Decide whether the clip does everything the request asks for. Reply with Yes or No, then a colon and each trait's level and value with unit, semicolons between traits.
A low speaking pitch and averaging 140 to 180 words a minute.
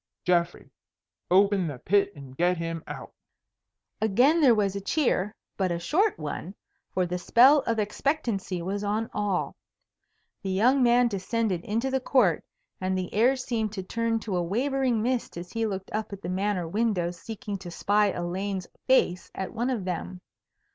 No: high, 200 Hz; average, 170 wpm